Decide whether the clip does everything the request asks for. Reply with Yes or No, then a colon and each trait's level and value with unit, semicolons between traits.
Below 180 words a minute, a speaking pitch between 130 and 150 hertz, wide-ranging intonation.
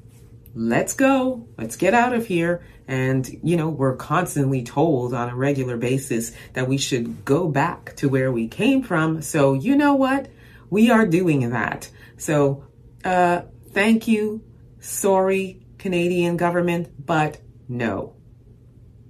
Yes: average, 140 wpm; medium, 140 Hz; wide, 6.6 semitones